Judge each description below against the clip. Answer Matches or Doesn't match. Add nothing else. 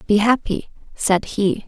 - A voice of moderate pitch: Doesn't match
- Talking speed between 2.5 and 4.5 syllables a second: Matches